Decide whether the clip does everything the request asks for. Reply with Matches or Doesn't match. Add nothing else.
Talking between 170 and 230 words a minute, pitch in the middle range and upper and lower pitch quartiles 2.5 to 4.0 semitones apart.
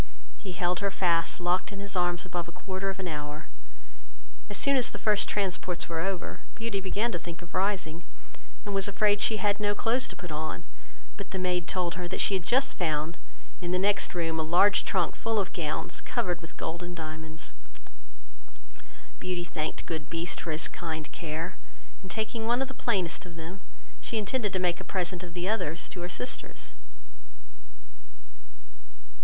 Matches